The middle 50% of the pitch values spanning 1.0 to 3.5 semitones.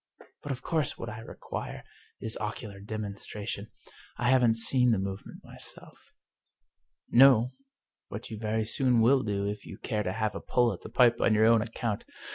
Yes: narrow, 2.5 semitones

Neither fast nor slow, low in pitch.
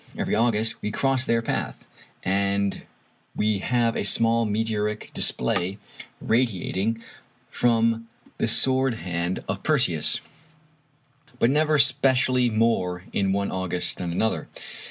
No: slow, 115 wpm; low, 115 Hz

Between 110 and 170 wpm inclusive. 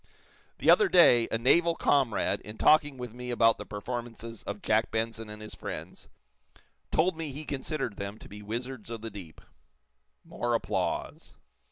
Yes: average, 165 wpm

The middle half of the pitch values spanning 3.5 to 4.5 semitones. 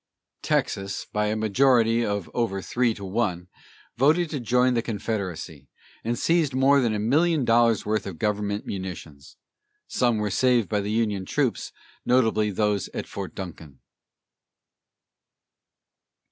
Yes: average, 3.8 semitones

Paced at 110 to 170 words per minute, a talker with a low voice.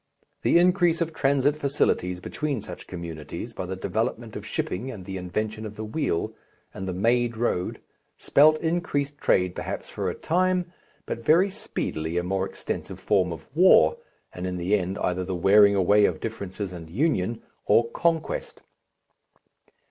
Yes: average, 160 wpm; low, 105 Hz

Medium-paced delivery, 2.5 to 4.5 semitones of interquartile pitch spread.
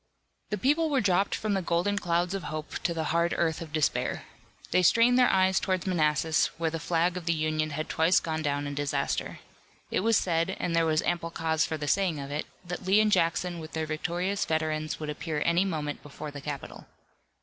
No: fast, 215 wpm; average, 3.1 semitones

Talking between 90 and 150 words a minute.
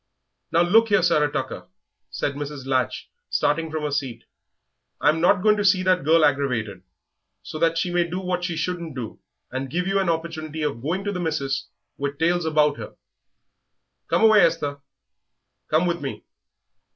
No: average, 175 wpm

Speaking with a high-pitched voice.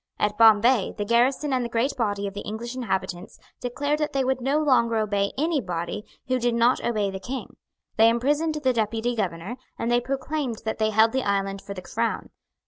Yes: high, 230 Hz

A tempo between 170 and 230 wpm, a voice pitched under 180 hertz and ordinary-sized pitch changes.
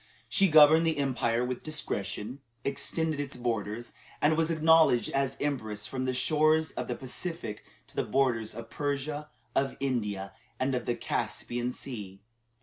No: average, 150 wpm; low, 135 Hz; average, 4.3 semitones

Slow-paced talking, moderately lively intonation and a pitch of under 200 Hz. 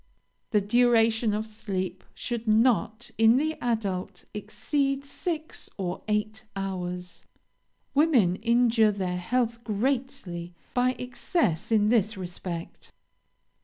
No: slow, 105 wpm; average, 4.2 semitones; high, 220 Hz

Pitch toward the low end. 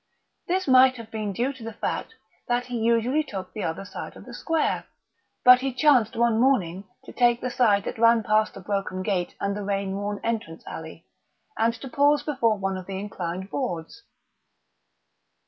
No: high, 225 Hz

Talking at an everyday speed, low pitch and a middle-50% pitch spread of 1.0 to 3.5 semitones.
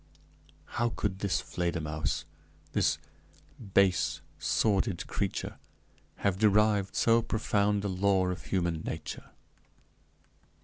No: slow, 95 wpm; low, 100 Hz; narrow, 2.4 semitones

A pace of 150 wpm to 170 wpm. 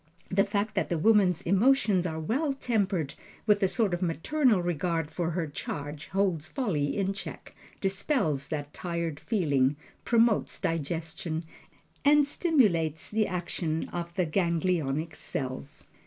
No: slow, 135 wpm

